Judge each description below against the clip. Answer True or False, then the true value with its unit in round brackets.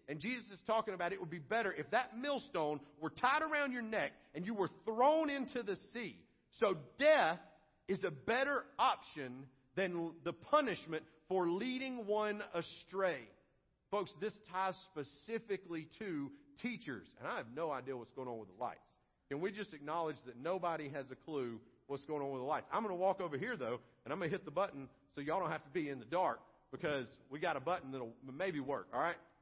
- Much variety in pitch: True (6.1 semitones)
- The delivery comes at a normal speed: False (210 wpm)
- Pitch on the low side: False (180 Hz)